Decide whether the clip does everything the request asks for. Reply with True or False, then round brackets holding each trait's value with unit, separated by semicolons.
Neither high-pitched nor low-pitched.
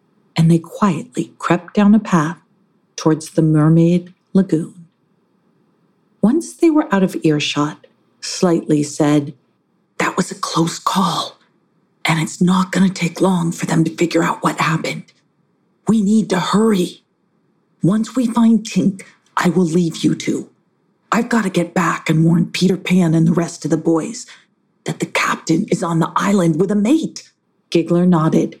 True (180 Hz)